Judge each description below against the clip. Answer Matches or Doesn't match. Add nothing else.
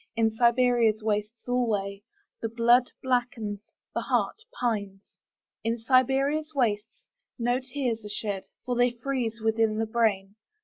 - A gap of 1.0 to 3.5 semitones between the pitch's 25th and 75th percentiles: Matches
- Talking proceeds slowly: Matches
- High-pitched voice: Matches